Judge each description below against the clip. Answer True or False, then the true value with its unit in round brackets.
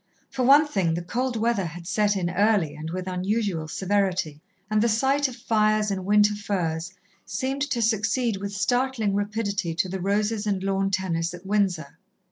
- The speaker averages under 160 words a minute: False (175 wpm)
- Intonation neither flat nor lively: True (3.2 semitones)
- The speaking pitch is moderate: False (200 Hz)